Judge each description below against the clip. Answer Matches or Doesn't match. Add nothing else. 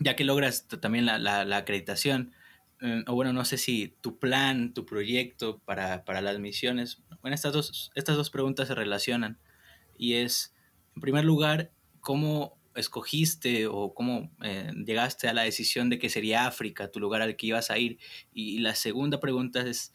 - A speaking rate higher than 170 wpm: Matches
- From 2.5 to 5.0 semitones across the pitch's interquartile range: Matches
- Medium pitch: Doesn't match